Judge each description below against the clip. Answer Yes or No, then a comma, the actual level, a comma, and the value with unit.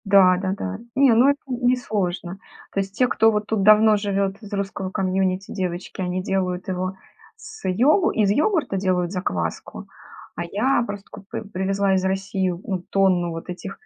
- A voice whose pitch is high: Yes, high, 195 Hz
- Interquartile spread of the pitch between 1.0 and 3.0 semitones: Yes, narrow, 2.4 semitones